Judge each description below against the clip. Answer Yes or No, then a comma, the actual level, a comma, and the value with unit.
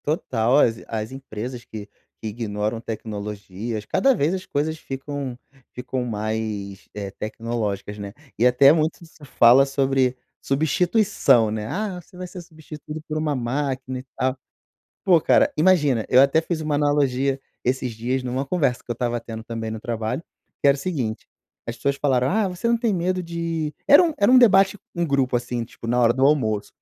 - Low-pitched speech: Yes, low, 130 Hz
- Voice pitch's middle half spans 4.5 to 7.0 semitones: Yes, wide, 5.5 semitones